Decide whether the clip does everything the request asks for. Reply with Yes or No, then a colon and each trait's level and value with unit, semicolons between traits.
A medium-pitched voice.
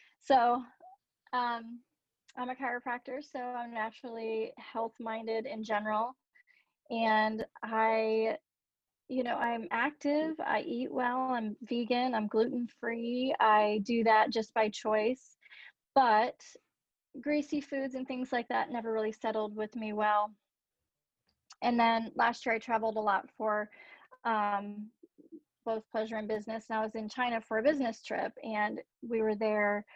No: high, 230 Hz